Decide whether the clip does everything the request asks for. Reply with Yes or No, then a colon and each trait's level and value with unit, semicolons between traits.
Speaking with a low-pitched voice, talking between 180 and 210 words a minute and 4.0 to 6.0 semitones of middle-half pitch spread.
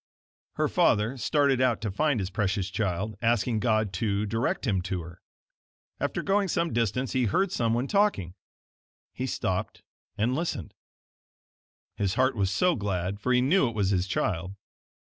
No: low, 110 Hz; average, 160 wpm; average, 5.0 semitones